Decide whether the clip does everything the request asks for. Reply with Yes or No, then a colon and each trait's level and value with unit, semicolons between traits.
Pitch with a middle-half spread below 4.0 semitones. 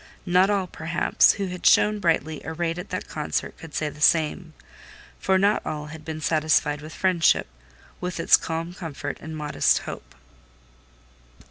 Yes: average, 3.0 semitones